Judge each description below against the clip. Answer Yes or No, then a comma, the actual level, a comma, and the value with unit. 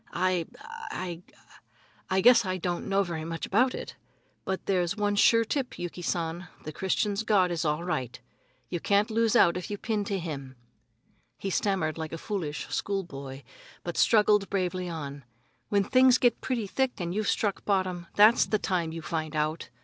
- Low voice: No, medium, 185 Hz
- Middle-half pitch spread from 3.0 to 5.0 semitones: Yes, average, 3.8 semitones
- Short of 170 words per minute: No, average, 175 wpm